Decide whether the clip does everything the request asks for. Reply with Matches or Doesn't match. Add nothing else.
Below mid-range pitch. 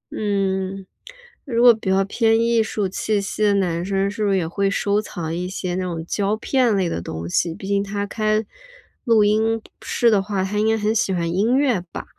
Doesn't match